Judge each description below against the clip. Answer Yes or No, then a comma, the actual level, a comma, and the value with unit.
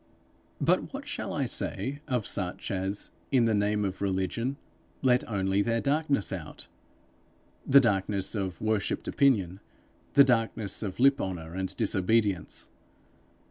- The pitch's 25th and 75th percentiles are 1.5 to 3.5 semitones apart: No, average, 4.4 semitones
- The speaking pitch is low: Yes, low, 105 Hz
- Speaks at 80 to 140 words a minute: Yes, slow, 135 wpm